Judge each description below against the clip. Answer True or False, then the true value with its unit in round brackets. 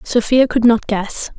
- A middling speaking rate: True (175 wpm)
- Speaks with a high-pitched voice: True (230 Hz)